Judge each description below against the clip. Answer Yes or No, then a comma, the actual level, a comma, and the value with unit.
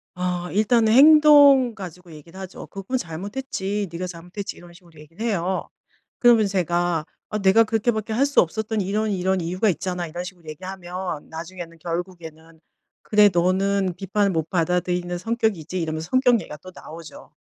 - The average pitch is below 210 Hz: Yes, medium, 185 Hz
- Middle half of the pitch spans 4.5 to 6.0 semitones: No, average, 3.7 semitones